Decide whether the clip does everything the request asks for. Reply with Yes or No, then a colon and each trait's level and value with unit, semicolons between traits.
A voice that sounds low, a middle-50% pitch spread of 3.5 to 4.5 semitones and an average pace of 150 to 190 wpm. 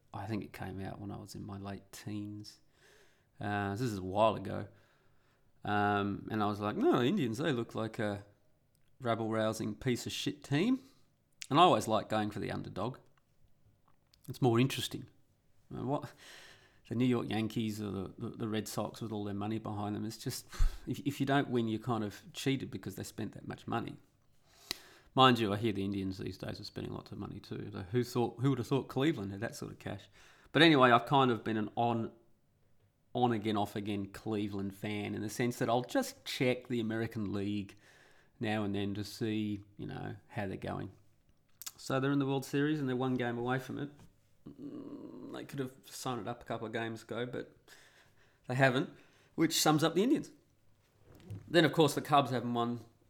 No: low, 115 Hz; average, 4.0 semitones; average, 200 wpm